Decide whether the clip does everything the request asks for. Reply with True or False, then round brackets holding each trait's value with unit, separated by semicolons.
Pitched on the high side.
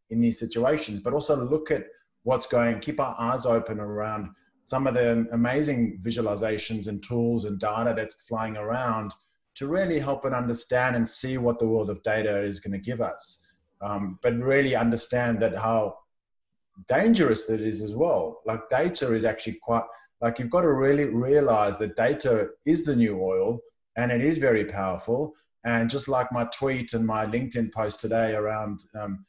False (115 Hz)